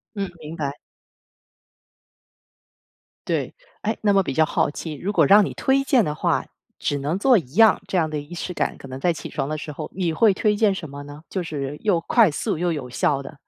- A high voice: No, medium, 165 Hz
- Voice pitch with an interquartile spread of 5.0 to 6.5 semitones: Yes, wide, 5.5 semitones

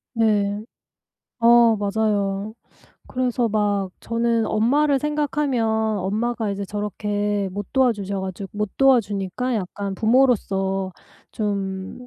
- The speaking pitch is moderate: No, high, 210 Hz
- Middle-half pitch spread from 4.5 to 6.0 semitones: No, average, 3.1 semitones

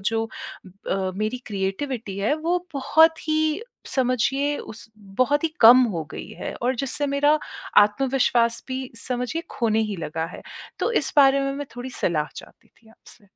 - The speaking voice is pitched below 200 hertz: No, very high, 250 Hz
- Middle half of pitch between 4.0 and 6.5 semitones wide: Yes, average, 4.8 semitones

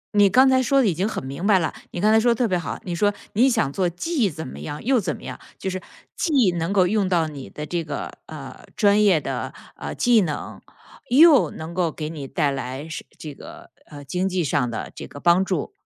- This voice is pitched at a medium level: Yes, medium, 180 Hz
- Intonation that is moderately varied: No, wide, 5.8 semitones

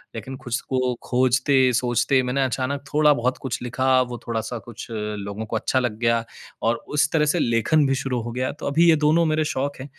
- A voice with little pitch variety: No, average, 3.0 semitones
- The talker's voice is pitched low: Yes, low, 130 Hz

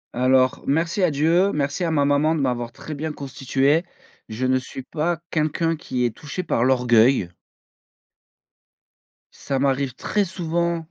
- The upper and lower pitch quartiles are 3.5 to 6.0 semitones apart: Yes, average, 4.0 semitones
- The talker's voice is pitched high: No, medium, 140 Hz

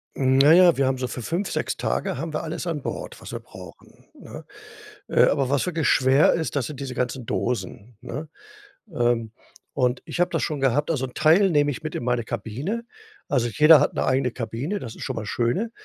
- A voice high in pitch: No, low, 135 Hz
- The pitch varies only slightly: No, average, 4.6 semitones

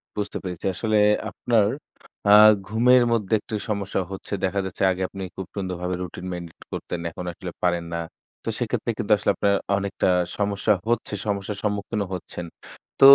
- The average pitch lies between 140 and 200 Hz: No, low, 100 Hz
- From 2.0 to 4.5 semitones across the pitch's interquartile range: Yes, narrow, 2.5 semitones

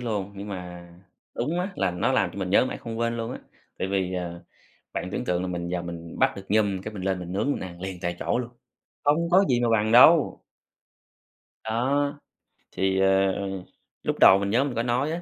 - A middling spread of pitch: Yes, average, 4.6 semitones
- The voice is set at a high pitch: No, low, 100 Hz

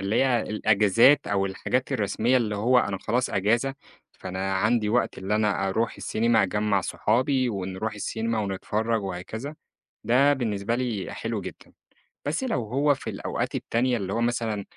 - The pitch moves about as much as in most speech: Yes, average, 3.6 semitones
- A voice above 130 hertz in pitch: No, low, 110 Hz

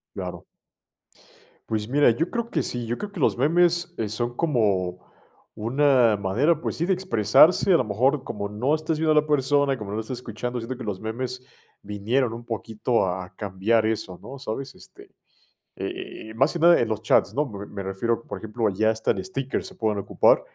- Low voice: Yes, low, 120 Hz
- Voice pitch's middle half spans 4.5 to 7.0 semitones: Yes, average, 5.1 semitones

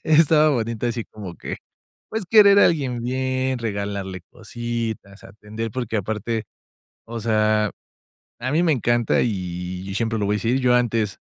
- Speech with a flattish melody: No, average, 3.4 semitones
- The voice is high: No, low, 115 Hz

